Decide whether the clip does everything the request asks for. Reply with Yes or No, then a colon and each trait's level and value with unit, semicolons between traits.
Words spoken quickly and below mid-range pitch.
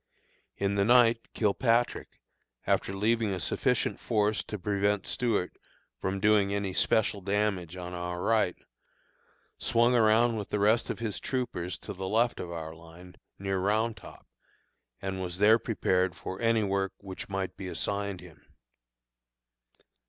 No: average, 145 wpm; low, 100 Hz